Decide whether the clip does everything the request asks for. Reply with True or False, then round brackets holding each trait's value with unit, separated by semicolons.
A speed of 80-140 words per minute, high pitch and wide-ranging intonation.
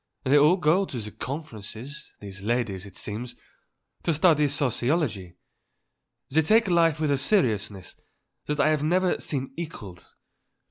False (135 wpm; 140 Hz; 6.6 semitones)